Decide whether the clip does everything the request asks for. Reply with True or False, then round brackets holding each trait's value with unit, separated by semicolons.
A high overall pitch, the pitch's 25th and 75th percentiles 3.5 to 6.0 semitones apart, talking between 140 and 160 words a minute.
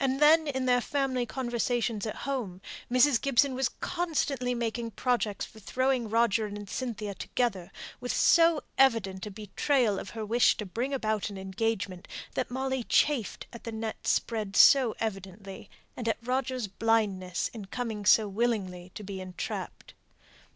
True (230 Hz; 4.0 semitones; 150 wpm)